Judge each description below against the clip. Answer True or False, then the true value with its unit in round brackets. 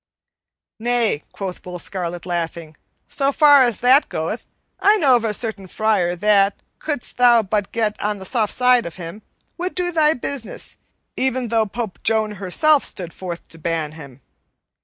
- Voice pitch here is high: True (215 Hz)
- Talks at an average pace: True (165 wpm)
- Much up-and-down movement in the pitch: True (5.7 semitones)